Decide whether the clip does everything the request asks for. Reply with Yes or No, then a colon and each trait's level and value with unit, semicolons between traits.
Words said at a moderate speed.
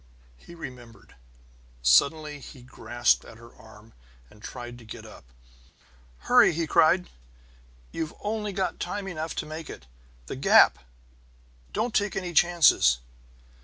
No: slow, 130 wpm